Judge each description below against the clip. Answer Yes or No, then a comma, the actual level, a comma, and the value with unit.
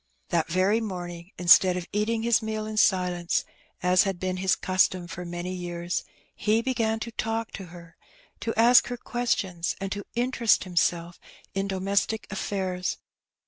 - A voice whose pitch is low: No, high, 190 Hz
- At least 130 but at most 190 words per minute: Yes, average, 160 wpm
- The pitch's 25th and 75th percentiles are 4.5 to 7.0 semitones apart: No, average, 3.8 semitones